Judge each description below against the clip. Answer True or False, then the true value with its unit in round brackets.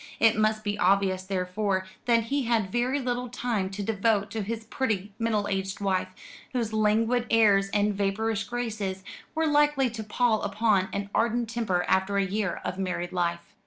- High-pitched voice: True (210 Hz)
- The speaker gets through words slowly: False (170 wpm)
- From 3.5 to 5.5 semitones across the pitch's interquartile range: False (2.9 semitones)